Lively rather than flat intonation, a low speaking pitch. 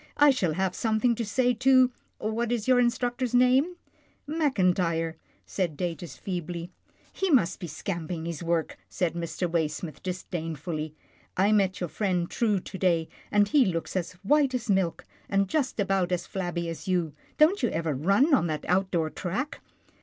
No: wide, 6.1 semitones; medium, 185 Hz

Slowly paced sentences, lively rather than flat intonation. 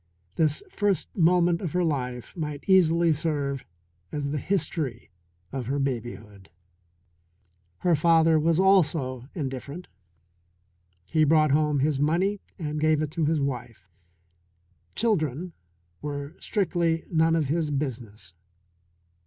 No: slow, 120 wpm; average, 3.4 semitones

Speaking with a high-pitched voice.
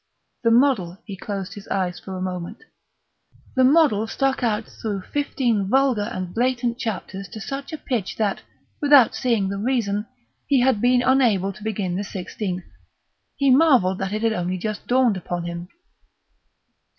Yes: high, 215 Hz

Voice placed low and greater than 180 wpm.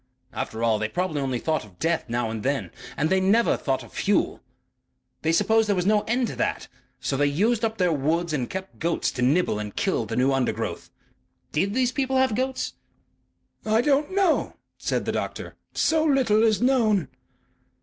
No: medium, 185 Hz; average, 190 wpm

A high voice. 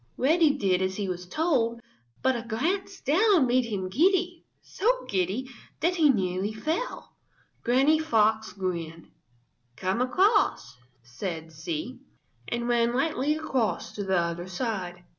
Yes: high, 235 Hz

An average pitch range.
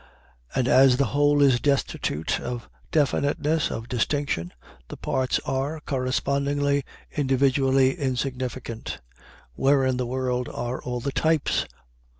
No: narrow, 2.2 semitones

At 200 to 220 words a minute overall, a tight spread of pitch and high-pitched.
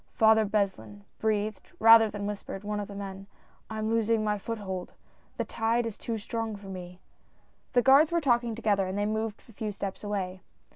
Yes: fast, 205 wpm; narrow, 2.1 semitones; high, 210 Hz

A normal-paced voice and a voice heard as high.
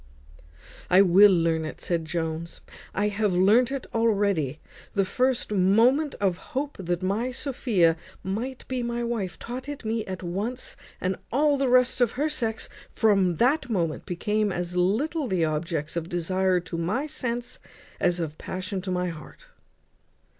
Yes: average, 160 wpm; high, 200 Hz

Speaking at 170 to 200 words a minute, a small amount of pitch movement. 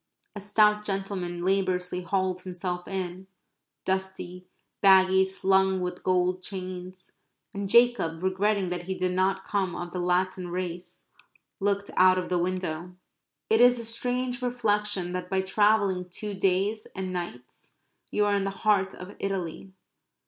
No: average, 145 wpm; narrow, 1.8 semitones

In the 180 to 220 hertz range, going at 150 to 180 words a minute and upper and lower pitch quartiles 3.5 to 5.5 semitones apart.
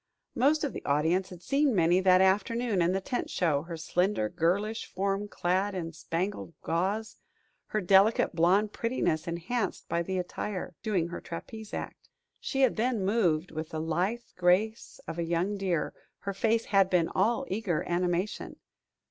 Yes: high, 190 Hz; average, 165 wpm; average, 3.8 semitones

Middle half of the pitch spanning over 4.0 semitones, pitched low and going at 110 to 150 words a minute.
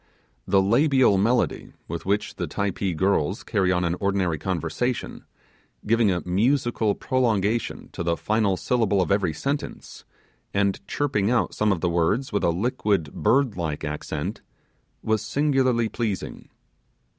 Yes: average, 4.6 semitones; low, 100 Hz; average, 140 wpm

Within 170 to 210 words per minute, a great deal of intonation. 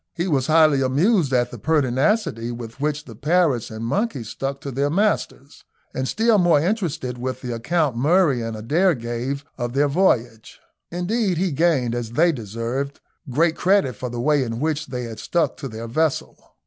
Yes: average, 180 wpm; wide, 5.7 semitones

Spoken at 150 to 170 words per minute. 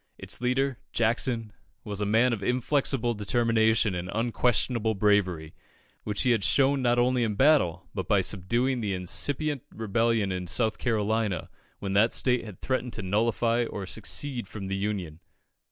Yes: average, 155 wpm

